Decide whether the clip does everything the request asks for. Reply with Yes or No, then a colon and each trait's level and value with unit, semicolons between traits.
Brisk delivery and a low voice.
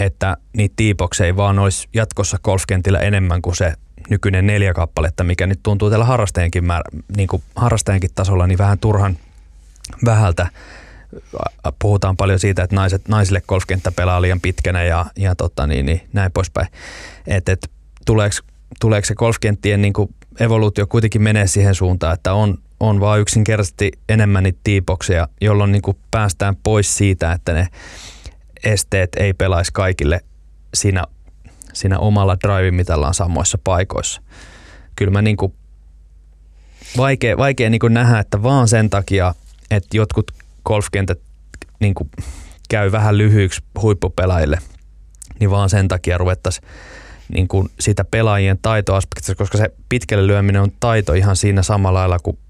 No: average, 140 wpm; very low, 95 Hz